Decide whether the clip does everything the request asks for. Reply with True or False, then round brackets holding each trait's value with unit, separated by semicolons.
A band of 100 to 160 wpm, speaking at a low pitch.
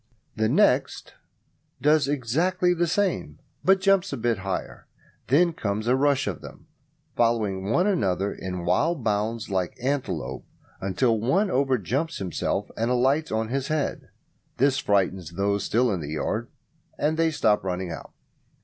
True (150 wpm; 120 Hz)